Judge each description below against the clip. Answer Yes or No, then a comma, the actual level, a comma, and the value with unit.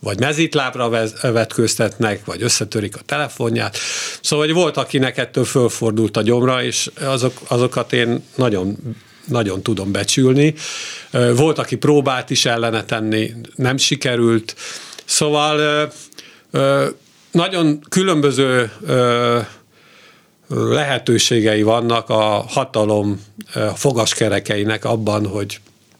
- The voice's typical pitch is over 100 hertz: Yes, low, 120 Hz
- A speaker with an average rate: No, slow, 95 wpm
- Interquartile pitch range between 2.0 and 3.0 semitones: No, average, 3.9 semitones